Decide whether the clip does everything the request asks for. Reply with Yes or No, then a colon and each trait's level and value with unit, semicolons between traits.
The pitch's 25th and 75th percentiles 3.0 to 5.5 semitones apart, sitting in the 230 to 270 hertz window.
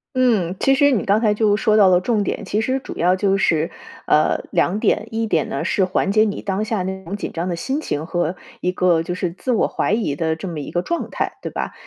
No: average, 3.8 semitones; high, 195 Hz